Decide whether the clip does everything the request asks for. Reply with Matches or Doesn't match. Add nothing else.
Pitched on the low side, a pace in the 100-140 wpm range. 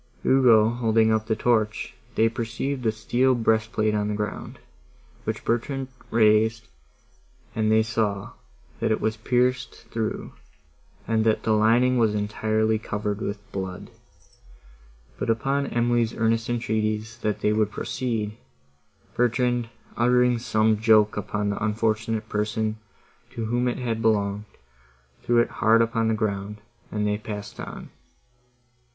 Matches